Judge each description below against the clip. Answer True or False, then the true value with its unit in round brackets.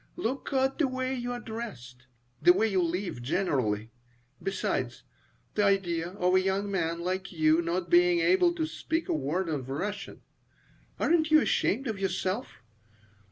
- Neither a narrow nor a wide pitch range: False (7.5 semitones)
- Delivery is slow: False (160 wpm)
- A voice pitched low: False (195 Hz)